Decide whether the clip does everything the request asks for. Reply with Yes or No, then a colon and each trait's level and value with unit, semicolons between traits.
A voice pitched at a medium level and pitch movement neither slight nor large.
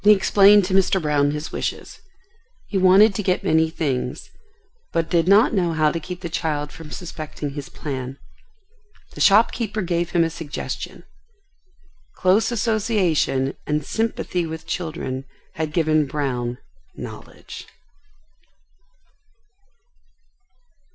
Yes: medium, 165 Hz; average, 4.3 semitones